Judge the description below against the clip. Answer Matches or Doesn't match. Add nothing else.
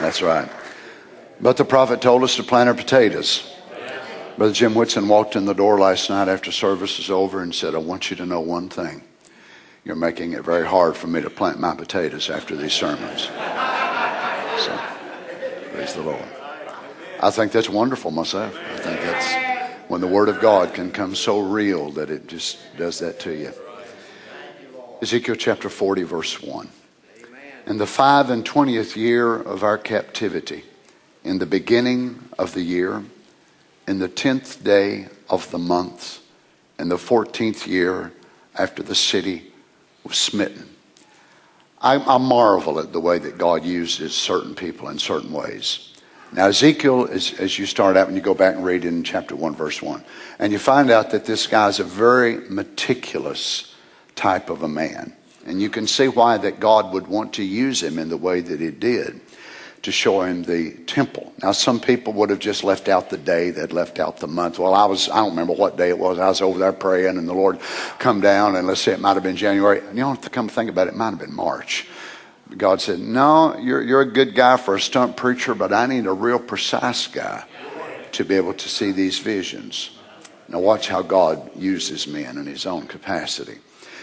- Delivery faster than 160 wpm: Matches